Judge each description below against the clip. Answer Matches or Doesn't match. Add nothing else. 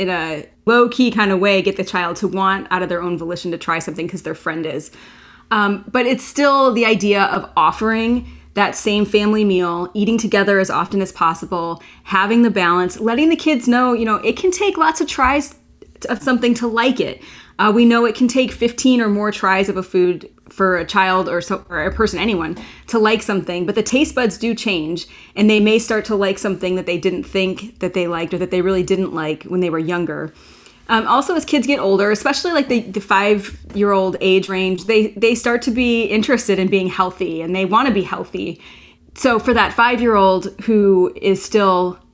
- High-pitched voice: Matches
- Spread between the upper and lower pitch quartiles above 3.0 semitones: Matches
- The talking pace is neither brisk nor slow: Doesn't match